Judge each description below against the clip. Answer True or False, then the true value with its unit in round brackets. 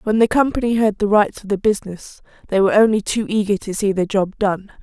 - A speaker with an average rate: False (235 wpm)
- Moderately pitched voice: False (205 Hz)